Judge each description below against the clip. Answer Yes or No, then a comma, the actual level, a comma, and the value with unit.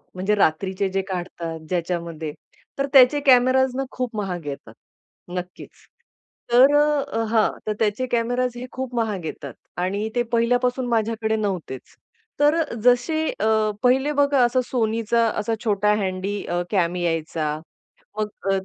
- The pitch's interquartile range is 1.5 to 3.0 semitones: No, average, 5.1 semitones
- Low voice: No, high, 220 Hz